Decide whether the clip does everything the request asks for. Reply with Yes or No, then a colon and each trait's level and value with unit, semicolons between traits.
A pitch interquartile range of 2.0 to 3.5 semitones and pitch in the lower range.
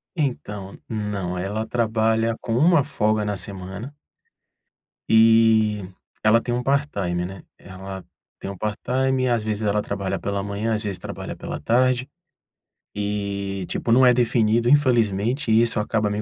Yes: average, 3.0 semitones; low, 110 Hz